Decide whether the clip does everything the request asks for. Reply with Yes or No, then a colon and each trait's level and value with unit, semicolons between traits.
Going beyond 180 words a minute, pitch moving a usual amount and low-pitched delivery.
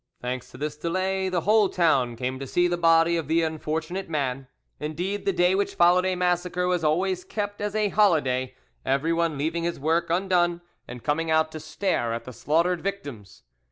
No: average, 190 wpm; average, 3.4 semitones; medium, 165 Hz